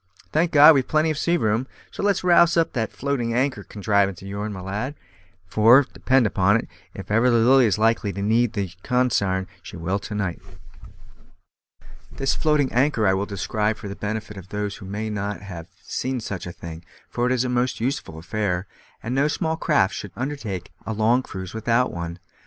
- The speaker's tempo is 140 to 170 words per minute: No, average, 200 wpm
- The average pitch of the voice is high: No, low, 110 Hz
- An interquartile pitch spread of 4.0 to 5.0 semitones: Yes, average, 4.6 semitones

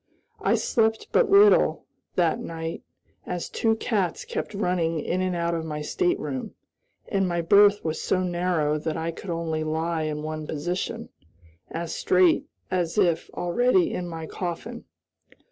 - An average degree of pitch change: Yes, average, 3.4 semitones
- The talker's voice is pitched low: No, medium, 175 Hz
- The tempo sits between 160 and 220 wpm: No, average, 150 wpm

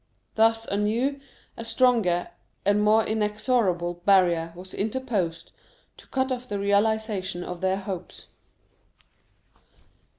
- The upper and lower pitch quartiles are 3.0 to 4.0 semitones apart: Yes, average, 3.5 semitones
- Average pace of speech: No, slow, 110 wpm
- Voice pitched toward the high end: Yes, high, 210 Hz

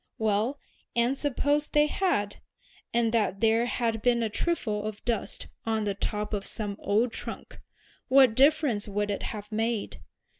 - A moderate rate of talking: Yes, average, 155 wpm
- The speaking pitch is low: No, high, 225 Hz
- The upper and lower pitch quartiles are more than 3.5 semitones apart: No, average, 3.2 semitones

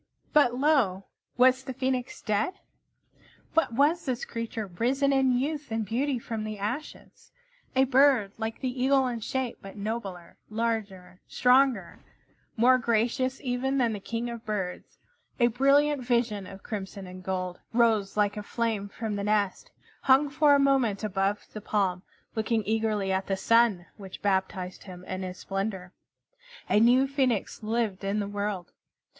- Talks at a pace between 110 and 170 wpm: Yes, average, 155 wpm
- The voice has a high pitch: Yes, high, 225 Hz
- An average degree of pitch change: Yes, average, 4.4 semitones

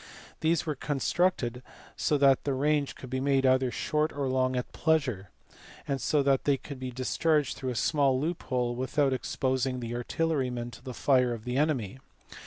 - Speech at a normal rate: Yes, average, 180 wpm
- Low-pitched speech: Yes, low, 130 Hz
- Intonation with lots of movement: No, narrow, 2.5 semitones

